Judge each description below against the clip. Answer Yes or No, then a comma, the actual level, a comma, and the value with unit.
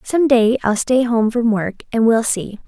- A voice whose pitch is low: No, high, 230 Hz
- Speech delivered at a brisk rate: Yes, fast, 225 wpm